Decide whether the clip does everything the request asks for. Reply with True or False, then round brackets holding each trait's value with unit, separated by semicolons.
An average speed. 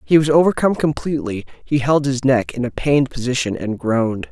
True (195 wpm)